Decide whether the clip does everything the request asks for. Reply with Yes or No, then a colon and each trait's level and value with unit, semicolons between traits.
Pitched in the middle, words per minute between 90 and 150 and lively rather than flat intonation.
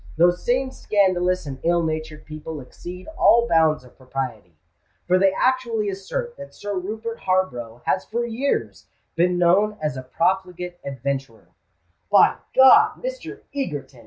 Yes: medium, 180 Hz; average, 140 wpm; wide, 6.2 semitones